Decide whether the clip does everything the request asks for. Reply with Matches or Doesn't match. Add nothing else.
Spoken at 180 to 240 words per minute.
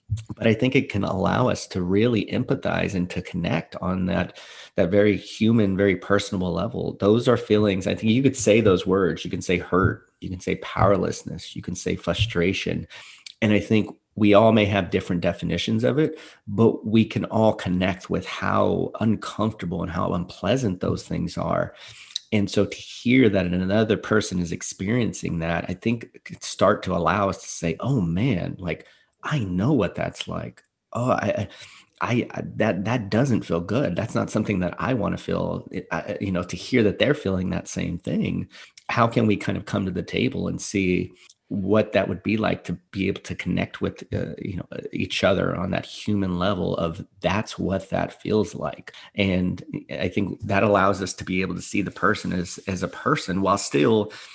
Matches